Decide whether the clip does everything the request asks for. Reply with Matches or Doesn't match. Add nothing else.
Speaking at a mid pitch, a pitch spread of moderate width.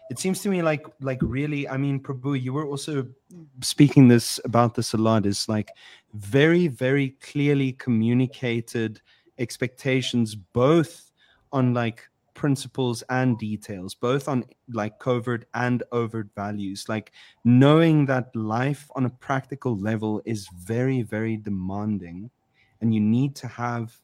Doesn't match